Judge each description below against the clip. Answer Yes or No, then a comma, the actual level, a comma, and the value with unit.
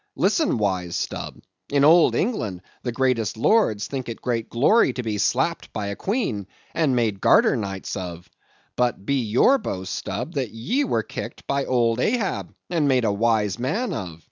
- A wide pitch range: Yes, wide, 5.7 semitones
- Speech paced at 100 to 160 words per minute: No, average, 175 wpm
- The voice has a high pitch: No, low, 120 Hz